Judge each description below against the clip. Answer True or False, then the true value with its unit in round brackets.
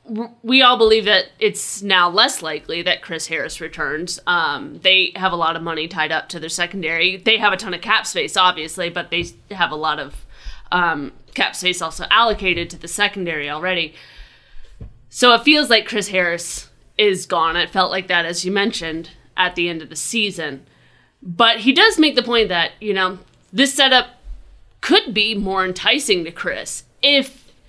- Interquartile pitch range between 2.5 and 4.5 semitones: False (4.9 semitones)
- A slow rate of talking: False (185 wpm)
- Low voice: False (185 Hz)